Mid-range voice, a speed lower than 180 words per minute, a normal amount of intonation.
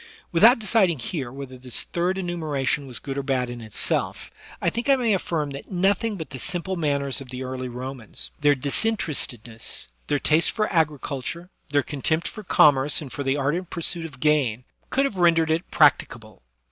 No: medium, 150 Hz; average, 185 wpm; average, 4.8 semitones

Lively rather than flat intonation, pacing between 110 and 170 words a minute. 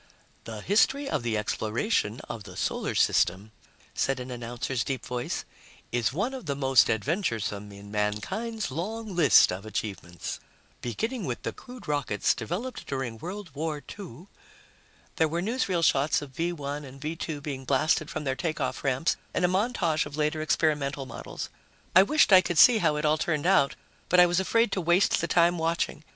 No: wide, 6.1 semitones; average, 180 wpm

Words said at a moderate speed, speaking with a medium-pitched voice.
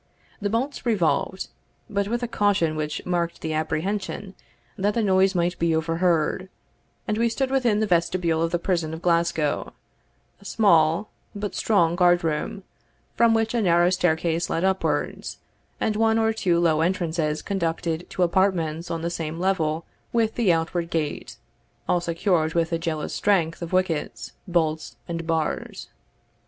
Yes: average, 155 wpm; medium, 175 Hz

